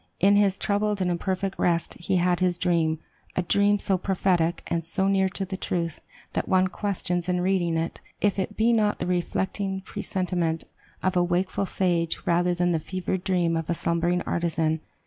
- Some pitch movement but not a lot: No, narrow, 2.1 semitones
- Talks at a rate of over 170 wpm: Yes, average, 185 wpm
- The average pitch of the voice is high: No, medium, 180 Hz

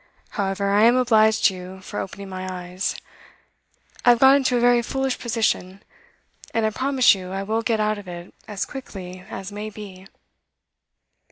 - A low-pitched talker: No, high, 210 Hz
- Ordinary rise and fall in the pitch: Yes, average, 3.8 semitones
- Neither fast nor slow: Yes, average, 175 wpm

